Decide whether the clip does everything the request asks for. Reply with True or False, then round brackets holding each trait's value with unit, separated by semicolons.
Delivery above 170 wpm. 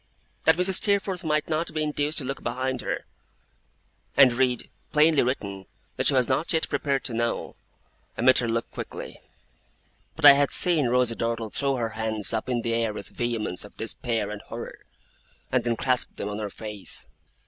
True (185 wpm)